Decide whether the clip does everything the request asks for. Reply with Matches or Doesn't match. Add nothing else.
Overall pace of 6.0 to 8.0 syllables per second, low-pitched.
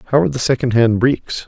Matches